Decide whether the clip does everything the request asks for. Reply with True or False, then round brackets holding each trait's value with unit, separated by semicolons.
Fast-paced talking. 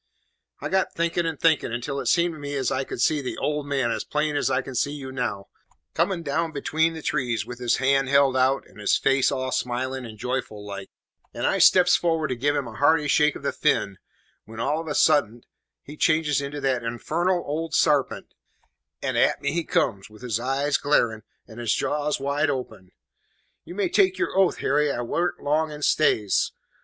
True (210 wpm)